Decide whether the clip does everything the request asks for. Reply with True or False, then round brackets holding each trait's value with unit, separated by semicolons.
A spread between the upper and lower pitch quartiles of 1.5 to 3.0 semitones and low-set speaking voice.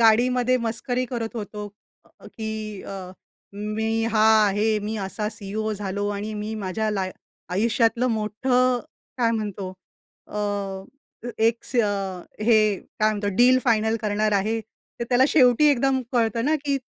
False (2.4 semitones; 220 Hz)